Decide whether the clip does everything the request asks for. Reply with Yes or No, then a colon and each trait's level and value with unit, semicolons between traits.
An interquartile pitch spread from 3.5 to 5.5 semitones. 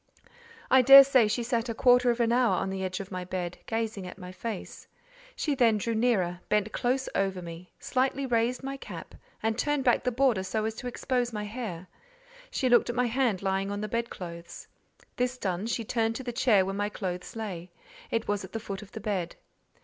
Yes: average, 4.3 semitones